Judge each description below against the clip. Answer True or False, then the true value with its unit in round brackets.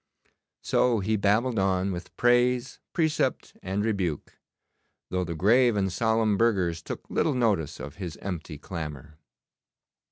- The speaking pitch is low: True (100 Hz)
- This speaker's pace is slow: True (130 wpm)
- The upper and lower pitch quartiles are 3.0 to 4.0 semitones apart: False (5.1 semitones)